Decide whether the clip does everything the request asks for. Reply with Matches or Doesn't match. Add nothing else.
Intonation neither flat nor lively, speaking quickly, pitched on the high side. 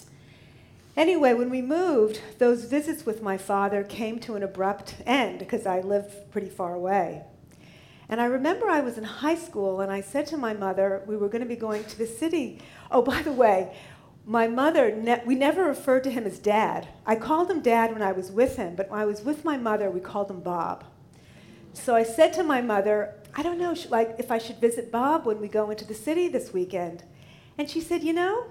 Doesn't match